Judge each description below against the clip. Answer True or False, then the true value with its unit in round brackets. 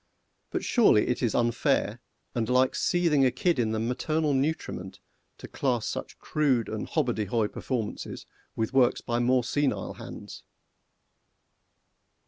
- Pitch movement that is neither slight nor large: True (4.0 semitones)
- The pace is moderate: False (130 wpm)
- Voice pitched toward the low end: True (125 Hz)